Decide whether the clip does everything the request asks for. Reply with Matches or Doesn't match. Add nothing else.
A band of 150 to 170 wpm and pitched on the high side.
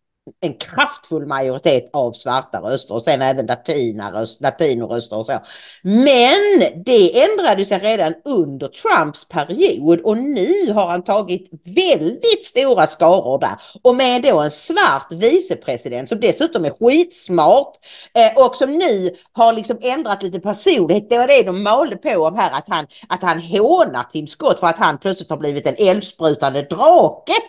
Matches